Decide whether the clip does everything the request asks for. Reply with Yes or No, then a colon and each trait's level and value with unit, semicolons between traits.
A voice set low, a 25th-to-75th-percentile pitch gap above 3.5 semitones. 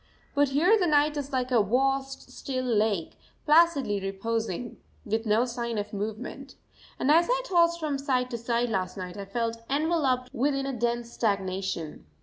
No: high, 245 Hz; average, 4.7 semitones